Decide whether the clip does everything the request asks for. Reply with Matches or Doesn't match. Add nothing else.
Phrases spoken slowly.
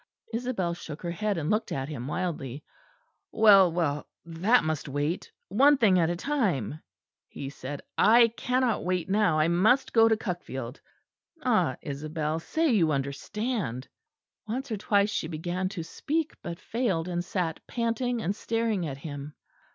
Doesn't match